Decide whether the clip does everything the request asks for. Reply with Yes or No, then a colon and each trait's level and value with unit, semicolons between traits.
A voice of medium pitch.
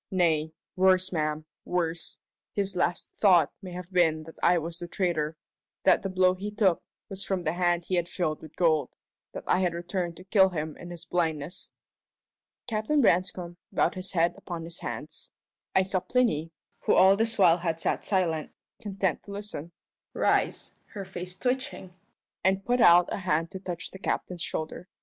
Yes: medium, 180 Hz